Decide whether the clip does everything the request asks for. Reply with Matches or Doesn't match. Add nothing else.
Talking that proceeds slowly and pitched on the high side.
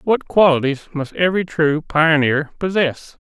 Doesn't match